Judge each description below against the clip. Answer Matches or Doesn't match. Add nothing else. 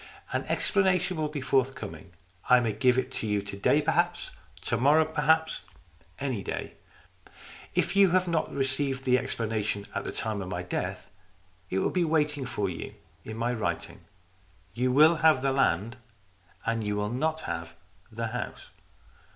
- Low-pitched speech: Matches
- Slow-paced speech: Doesn't match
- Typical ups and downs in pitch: Doesn't match